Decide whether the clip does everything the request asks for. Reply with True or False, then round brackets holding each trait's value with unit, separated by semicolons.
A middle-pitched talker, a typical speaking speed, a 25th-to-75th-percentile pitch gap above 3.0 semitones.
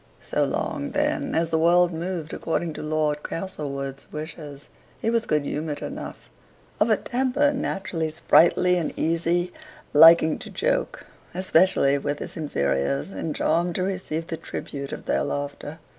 True (165 Hz; 150 wpm; 3.8 semitones)